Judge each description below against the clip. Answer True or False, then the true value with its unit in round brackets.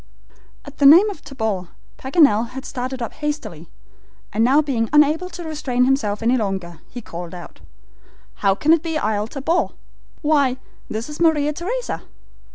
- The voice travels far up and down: True (5.7 semitones)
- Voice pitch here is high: True (265 Hz)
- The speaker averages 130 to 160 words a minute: True (155 wpm)